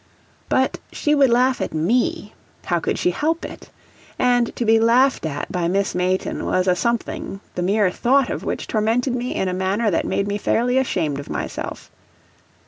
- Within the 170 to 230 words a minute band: Yes, average, 185 wpm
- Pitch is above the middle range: Yes, high, 215 Hz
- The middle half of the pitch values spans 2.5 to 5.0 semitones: No, wide, 5.4 semitones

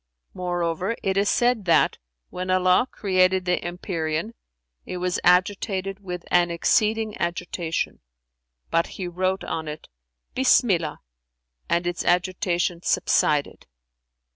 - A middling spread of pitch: No, narrow, 1.9 semitones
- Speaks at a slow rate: Yes, slow, 115 wpm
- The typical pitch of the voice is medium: Yes, medium, 180 Hz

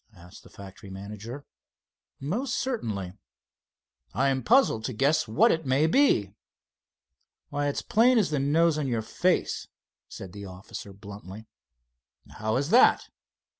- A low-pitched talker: Yes, low, 130 Hz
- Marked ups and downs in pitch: Yes, wide, 7.7 semitones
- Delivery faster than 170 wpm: No, slow, 135 wpm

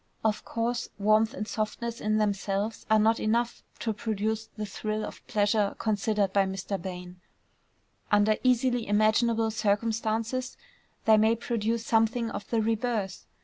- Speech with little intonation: Yes, narrow, 1.6 semitones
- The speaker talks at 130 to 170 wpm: Yes, average, 140 wpm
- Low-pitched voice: No, high, 220 Hz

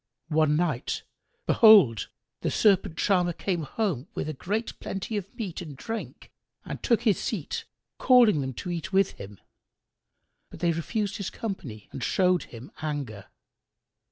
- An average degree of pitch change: No, wide, 5.9 semitones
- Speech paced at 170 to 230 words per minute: No, average, 145 wpm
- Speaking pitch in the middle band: Yes, medium, 175 Hz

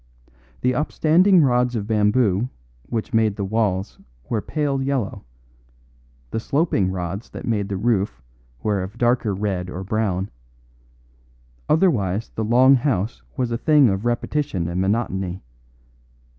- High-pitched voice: No, low, 110 Hz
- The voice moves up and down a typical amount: Yes, average, 4.6 semitones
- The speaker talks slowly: Yes, slow, 130 wpm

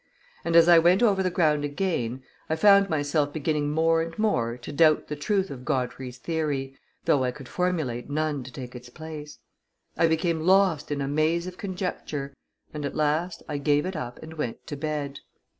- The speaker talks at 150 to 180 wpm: No, average, 190 wpm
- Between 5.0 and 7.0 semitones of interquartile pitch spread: No, average, 3.1 semitones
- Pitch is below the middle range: No, medium, 155 Hz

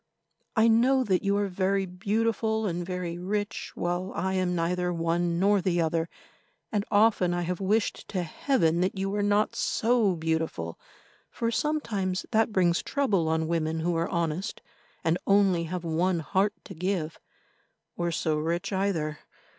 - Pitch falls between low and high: Yes, medium, 180 Hz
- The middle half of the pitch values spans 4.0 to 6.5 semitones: No, average, 3.3 semitones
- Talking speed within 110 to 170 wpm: Yes, average, 160 wpm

